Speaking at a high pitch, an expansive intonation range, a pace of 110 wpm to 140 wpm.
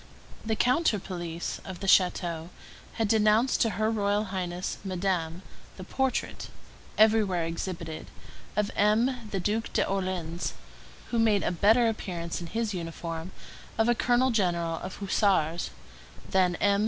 No: high, 195 Hz; average, 4.0 semitones; slow, 135 wpm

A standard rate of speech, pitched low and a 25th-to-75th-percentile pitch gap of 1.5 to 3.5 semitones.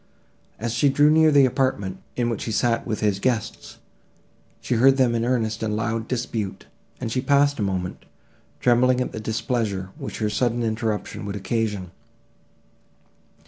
Yes: average, 160 wpm; low, 115 Hz; average, 3.1 semitones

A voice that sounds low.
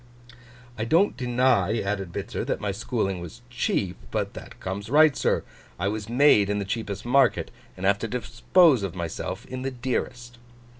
Yes: low, 115 Hz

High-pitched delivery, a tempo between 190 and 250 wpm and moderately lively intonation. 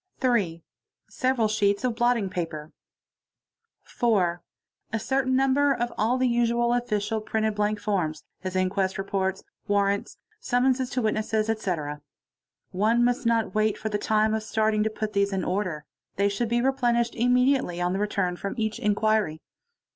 No: high, 215 Hz; average, 155 wpm; average, 3.2 semitones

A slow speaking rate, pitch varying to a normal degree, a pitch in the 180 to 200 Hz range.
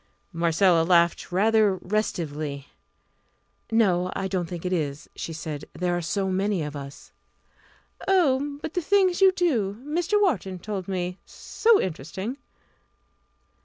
No: slow, 130 wpm; wide, 7.3 semitones; high, 190 Hz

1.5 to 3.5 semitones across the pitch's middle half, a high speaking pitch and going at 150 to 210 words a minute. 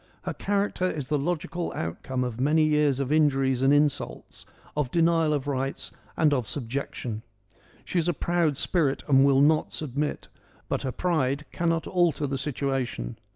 No: average, 3.1 semitones; medium, 145 Hz; average, 160 wpm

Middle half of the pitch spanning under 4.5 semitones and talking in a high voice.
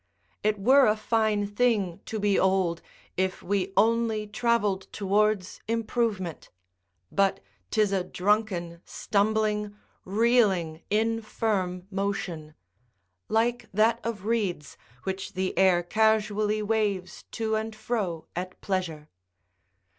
Yes: average, 2.7 semitones; high, 205 Hz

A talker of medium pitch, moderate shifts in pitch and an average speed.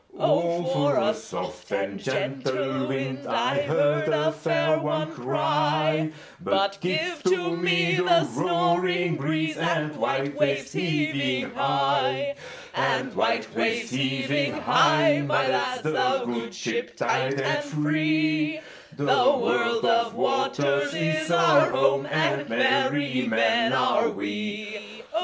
No: medium, 155 Hz; average, 4.4 semitones; slow, 100 wpm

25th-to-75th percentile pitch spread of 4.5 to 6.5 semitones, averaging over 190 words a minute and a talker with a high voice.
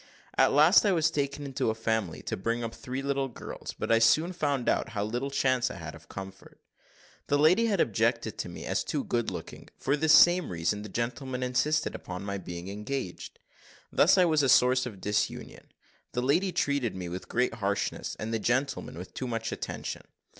No: wide, 5.4 semitones; average, 200 wpm; low, 125 Hz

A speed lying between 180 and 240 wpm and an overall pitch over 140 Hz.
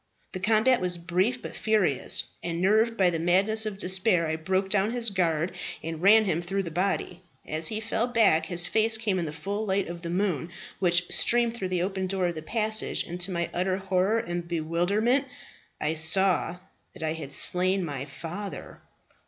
Yes: average, 195 wpm; medium, 185 Hz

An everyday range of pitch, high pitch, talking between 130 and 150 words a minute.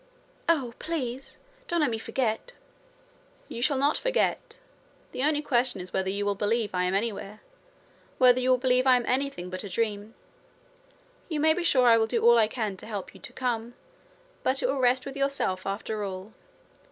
No: average, 4.4 semitones; high, 240 Hz; average, 190 wpm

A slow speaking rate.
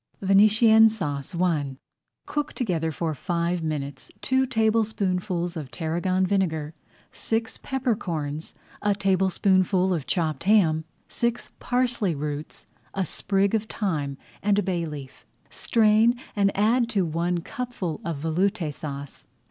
Yes: slow, 125 wpm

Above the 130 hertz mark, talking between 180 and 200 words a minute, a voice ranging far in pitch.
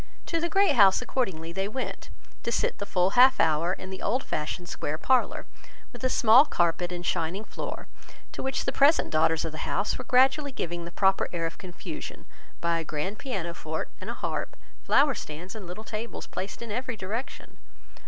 Yes: high, 190 Hz; average, 195 wpm; wide, 6.7 semitones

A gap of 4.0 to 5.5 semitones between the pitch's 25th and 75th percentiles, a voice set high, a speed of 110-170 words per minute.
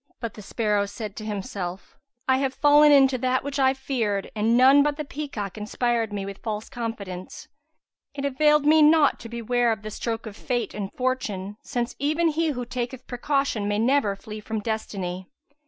No: average, 4.7 semitones; high, 235 Hz; average, 185 wpm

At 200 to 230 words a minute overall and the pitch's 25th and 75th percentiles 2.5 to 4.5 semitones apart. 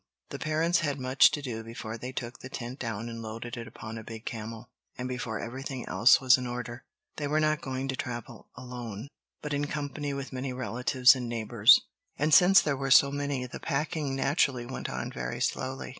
Yes: fast, 205 wpm; average, 3.0 semitones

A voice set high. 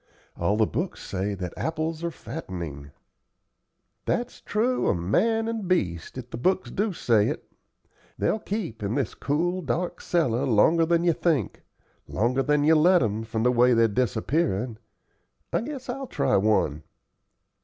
No: low, 135 Hz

